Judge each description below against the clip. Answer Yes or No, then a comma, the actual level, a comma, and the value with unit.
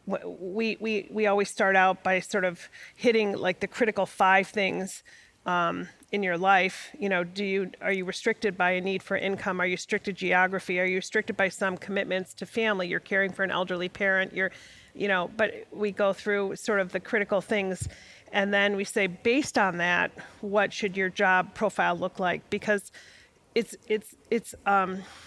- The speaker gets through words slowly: No, average, 190 wpm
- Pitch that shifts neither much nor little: No, narrow, 1.9 semitones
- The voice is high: Yes, high, 195 Hz